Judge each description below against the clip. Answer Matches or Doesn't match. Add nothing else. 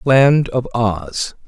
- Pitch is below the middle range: Matches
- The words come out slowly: Matches